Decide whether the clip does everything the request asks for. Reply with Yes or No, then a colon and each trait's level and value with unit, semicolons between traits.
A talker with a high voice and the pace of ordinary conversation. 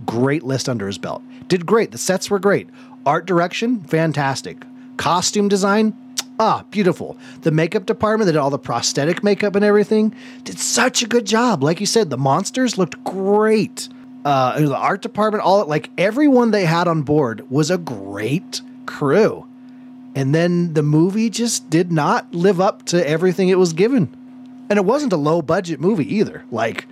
Yes: high, 200 Hz; average, 180 wpm